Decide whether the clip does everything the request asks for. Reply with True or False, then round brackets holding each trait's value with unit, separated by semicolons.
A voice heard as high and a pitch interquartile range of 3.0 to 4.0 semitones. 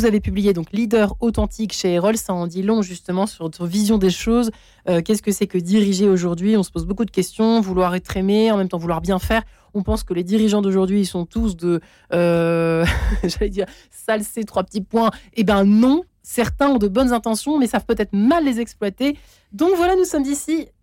True (210 Hz; 3.3 semitones)